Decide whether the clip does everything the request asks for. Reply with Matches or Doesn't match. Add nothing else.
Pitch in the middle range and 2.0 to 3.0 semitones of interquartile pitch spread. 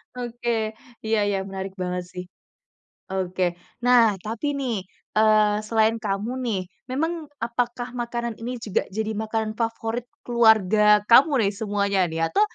Doesn't match